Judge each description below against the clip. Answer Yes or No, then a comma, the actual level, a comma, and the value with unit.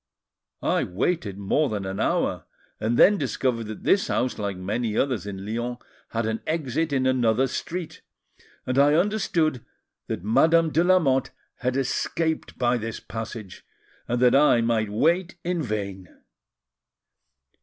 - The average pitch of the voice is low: Yes, low, 125 Hz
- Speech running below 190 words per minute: Yes, average, 145 wpm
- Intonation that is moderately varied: No, wide, 6.2 semitones